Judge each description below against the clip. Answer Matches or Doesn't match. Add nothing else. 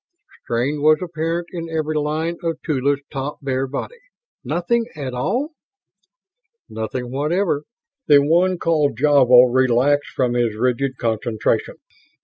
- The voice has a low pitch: Doesn't match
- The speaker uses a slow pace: Matches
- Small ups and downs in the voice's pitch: Doesn't match